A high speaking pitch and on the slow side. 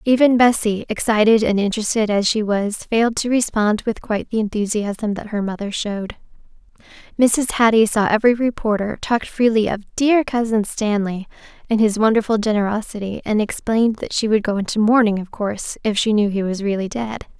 No: high, 215 Hz; average, 175 wpm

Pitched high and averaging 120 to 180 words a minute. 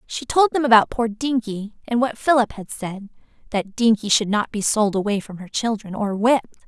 No: high, 225 Hz; fast, 205 wpm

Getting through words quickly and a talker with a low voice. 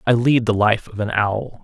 Yes: fast, 260 wpm; low, 110 Hz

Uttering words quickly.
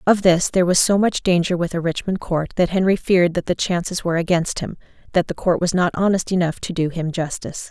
Yes: fast, 240 wpm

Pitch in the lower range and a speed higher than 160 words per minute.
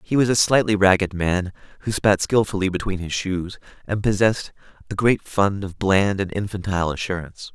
Yes: low, 100 Hz; average, 175 wpm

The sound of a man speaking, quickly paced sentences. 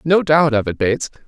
Yes: male; fast, 235 wpm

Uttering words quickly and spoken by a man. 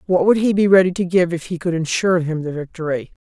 No: fast, 260 wpm; female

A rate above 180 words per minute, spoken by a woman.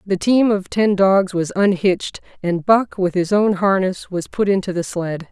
Yes: fast, 205 wpm; female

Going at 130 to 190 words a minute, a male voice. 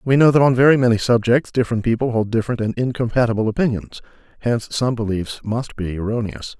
Yes: average, 180 wpm; male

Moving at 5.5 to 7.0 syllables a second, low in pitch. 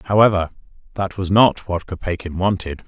No: 5.0 syllables/s; very low, 95 Hz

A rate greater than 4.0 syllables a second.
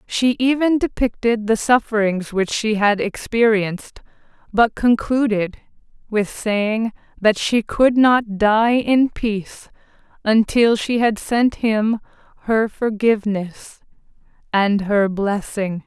No: 3.6 syllables/s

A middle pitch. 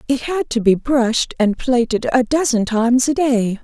No: high, 245 Hz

